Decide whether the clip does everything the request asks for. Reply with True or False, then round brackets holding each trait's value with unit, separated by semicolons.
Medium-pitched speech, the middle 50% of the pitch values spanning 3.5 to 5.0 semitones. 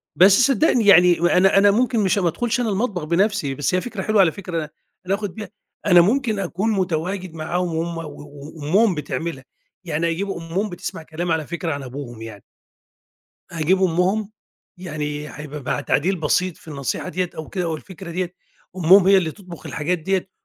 True (175 Hz; 3.8 semitones)